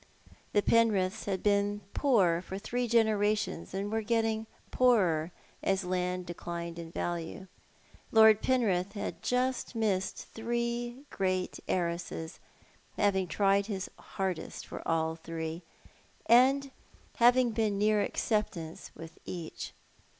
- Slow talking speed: Yes, slow, 115 wpm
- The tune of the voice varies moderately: Yes, average, 4.0 semitones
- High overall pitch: Yes, high, 200 Hz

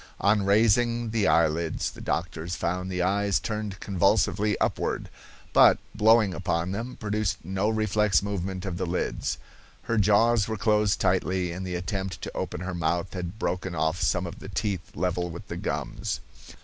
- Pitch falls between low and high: No, very low, 95 Hz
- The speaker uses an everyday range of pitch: Yes, average, 3.1 semitones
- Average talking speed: Yes, average, 165 wpm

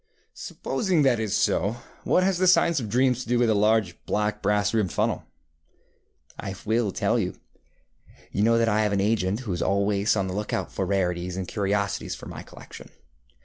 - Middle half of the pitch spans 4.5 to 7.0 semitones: No, average, 2.8 semitones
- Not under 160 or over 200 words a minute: Yes, average, 195 wpm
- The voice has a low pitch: Yes, low, 105 Hz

